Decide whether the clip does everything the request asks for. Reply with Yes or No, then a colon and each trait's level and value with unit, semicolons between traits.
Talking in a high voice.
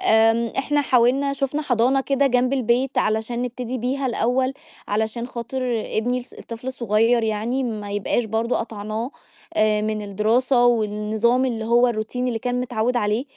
Yes: high, 235 Hz